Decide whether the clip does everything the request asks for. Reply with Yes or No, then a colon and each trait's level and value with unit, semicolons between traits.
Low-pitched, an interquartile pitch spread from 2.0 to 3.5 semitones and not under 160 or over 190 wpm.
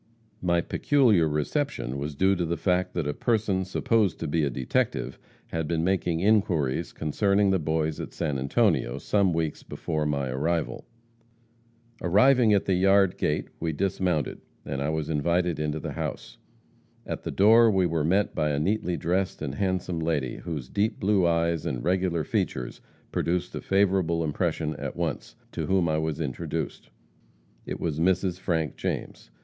No: very low, 85 Hz; average, 3.9 semitones; average, 165 wpm